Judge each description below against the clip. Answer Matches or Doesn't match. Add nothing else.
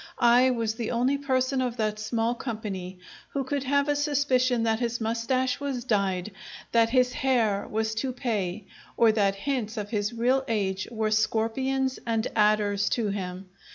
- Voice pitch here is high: Matches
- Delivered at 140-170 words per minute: Matches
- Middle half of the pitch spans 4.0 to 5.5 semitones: Doesn't match